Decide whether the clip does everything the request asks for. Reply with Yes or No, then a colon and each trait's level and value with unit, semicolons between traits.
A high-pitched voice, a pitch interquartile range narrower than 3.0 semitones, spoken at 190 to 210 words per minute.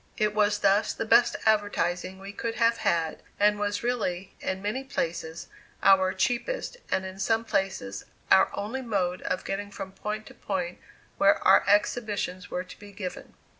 No: high, 200 Hz; narrow, 2.4 semitones; average, 170 wpm